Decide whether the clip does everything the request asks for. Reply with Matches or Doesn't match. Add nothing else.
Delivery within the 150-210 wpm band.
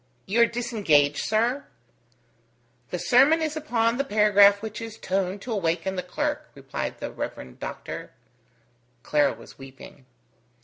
Doesn't match